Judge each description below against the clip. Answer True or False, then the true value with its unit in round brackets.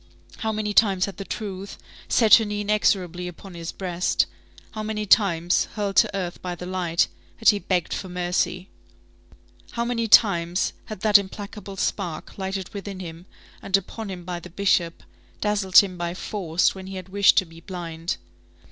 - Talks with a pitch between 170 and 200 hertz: True (190 Hz)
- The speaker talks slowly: False (175 wpm)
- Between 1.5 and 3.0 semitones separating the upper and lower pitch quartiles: True (2.6 semitones)